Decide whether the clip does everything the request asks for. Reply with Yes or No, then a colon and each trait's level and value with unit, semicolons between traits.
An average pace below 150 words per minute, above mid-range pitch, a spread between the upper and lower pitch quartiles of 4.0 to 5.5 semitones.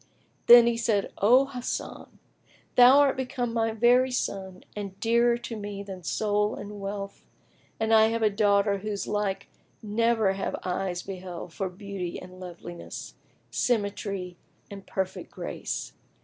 No: average, 140 wpm; high, 205 Hz; average, 3.1 semitones